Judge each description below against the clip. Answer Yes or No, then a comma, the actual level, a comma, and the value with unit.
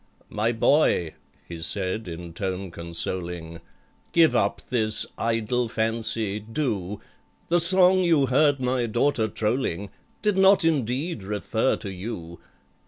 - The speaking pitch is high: No, low, 110 Hz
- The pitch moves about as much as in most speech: No, wide, 6.3 semitones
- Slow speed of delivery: Yes, slow, 115 wpm